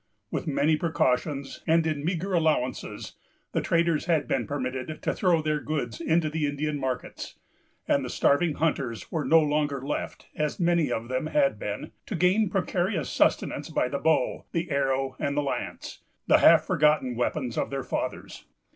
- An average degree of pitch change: Yes, average, 3.3 semitones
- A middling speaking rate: Yes, average, 165 wpm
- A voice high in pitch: No, medium, 150 Hz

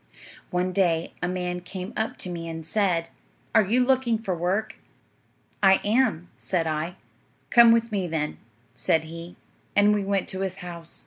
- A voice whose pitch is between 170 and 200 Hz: Yes, medium, 185 Hz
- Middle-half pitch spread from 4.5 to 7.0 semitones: No, average, 3.7 semitones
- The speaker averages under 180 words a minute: Yes, average, 170 wpm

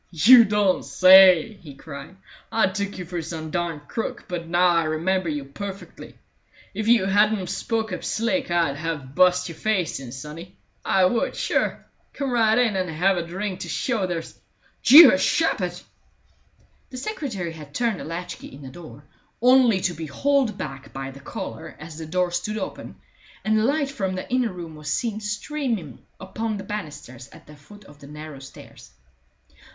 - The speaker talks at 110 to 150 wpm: No, average, 180 wpm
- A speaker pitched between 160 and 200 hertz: Yes, medium, 185 Hz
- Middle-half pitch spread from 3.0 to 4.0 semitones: No, wide, 5.4 semitones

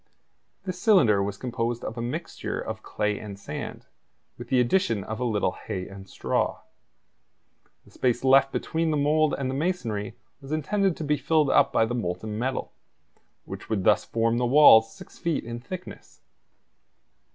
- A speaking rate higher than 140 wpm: Yes, average, 170 wpm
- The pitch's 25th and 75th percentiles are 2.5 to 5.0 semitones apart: No, wide, 5.5 semitones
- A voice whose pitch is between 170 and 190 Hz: No, low, 125 Hz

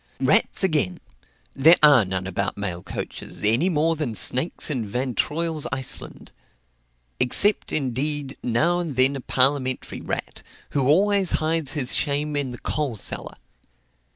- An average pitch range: Yes, average, 4.0 semitones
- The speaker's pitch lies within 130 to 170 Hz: Yes, medium, 140 Hz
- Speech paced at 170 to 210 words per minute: No, average, 140 wpm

